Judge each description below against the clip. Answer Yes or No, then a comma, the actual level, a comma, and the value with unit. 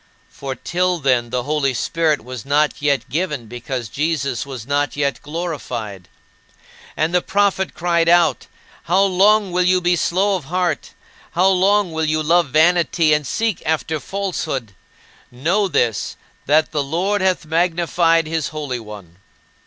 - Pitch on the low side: No, medium, 160 Hz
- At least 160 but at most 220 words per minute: No, average, 150 wpm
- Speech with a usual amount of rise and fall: Yes, average, 4.5 semitones